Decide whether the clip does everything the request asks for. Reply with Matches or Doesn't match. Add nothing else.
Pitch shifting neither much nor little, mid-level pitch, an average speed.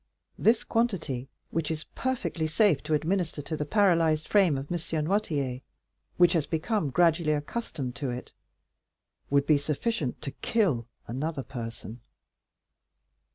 Doesn't match